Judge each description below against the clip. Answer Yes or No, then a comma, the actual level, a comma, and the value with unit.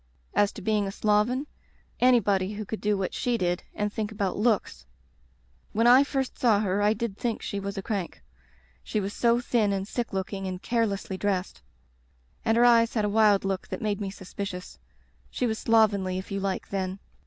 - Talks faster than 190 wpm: Yes, average, 200 wpm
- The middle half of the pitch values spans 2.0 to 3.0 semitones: Yes, average, 2.7 semitones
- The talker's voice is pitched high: Yes, high, 205 Hz